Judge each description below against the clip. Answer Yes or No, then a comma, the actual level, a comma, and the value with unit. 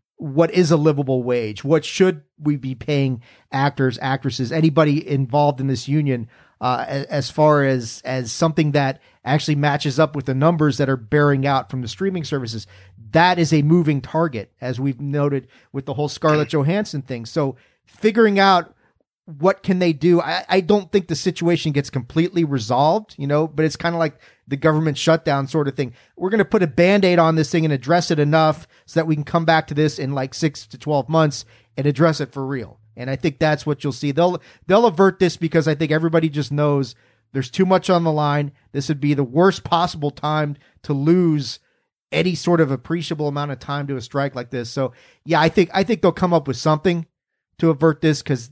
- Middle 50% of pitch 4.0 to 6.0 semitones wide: No, average, 3.3 semitones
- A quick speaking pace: Yes, fast, 215 wpm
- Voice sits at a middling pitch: Yes, medium, 150 Hz